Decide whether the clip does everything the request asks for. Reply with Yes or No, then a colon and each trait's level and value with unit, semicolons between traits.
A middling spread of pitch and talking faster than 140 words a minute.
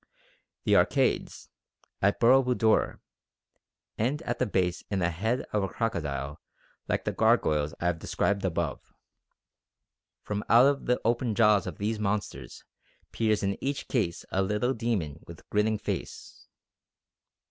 No: average, 5.0 semitones; slow, 135 wpm